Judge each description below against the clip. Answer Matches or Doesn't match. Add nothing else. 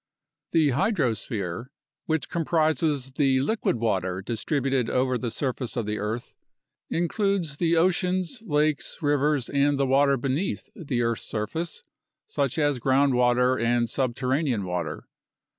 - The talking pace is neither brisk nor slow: Doesn't match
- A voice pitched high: Doesn't match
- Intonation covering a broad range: Doesn't match